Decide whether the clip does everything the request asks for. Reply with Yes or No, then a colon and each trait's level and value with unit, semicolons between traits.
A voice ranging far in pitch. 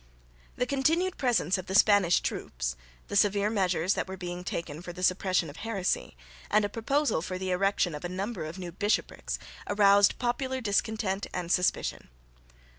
No: average, 3.2 semitones